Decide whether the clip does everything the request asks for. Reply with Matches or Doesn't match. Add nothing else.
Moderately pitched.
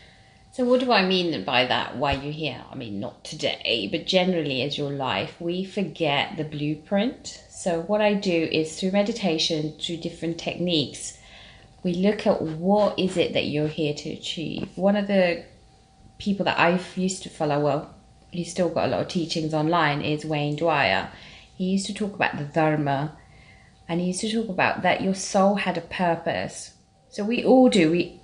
Matches